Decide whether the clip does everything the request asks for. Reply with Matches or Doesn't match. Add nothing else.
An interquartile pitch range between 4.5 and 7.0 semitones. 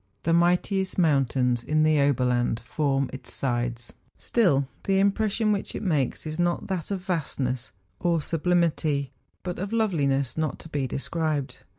Matches